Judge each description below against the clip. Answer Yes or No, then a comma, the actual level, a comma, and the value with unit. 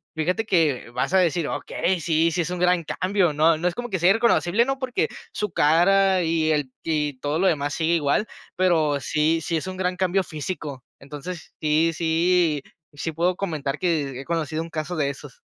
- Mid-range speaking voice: Yes, medium, 165 Hz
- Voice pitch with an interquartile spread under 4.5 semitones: Yes, average, 3.1 semitones